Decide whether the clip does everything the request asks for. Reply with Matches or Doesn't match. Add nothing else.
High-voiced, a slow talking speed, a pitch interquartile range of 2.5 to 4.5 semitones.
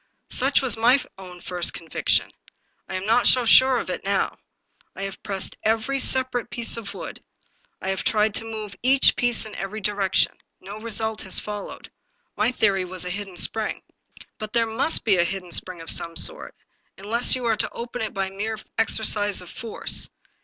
Doesn't match